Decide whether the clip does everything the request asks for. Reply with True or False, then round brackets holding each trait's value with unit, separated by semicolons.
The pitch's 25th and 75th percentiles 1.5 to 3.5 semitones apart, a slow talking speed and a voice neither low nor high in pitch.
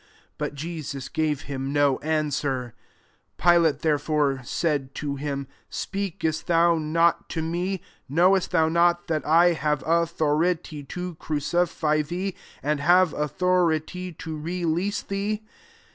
True (2.8 semitones; 130 wpm; 160 Hz)